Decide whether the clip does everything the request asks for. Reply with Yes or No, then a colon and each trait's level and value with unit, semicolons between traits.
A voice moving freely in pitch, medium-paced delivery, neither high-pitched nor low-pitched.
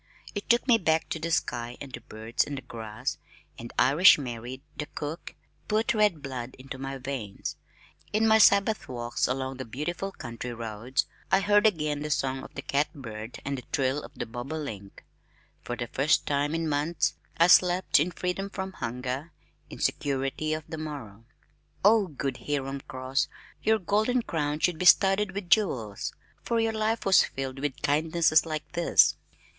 Yes: wide, 5.7 semitones; average, 175 wpm; medium, 145 Hz